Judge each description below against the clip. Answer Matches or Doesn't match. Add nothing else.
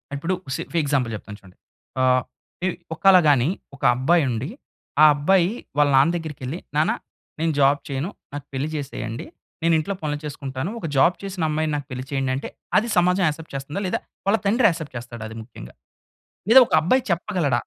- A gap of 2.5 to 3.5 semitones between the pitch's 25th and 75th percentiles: Doesn't match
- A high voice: Doesn't match